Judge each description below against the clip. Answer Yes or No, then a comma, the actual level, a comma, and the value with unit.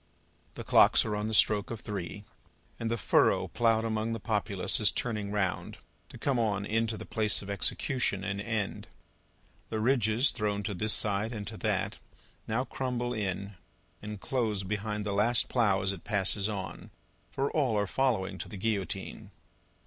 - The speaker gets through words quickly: No, average, 170 wpm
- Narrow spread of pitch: Yes, narrow, 2.2 semitones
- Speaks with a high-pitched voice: No, low, 105 Hz